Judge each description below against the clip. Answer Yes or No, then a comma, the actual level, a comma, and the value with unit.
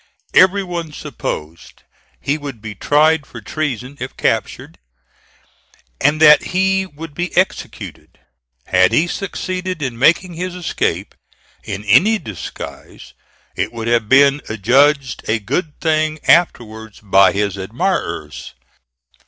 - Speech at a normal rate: No, slow, 120 wpm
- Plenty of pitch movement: Yes, wide, 7.4 semitones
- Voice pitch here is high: No, medium, 145 Hz